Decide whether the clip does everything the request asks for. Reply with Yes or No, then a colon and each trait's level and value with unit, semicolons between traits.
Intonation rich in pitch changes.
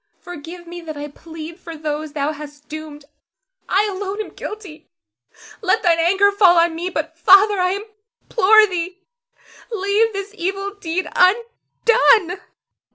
No: average, 3.7 semitones